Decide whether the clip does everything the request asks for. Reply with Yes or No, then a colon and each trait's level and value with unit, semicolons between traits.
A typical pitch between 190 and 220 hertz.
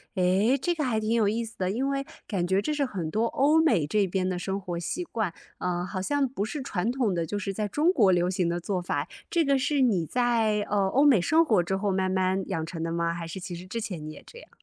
Yes: high, 200 Hz